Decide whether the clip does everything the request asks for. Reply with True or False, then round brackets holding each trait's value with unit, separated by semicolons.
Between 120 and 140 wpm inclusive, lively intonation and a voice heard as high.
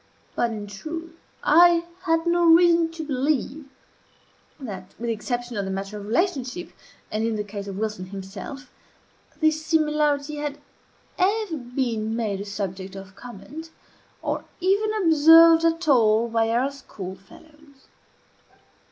True (135 wpm; 7.4 semitones; 270 Hz)